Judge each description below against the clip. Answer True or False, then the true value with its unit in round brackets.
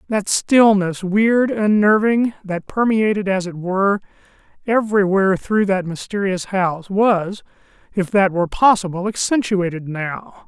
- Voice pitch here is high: True (200 Hz)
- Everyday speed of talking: False (120 wpm)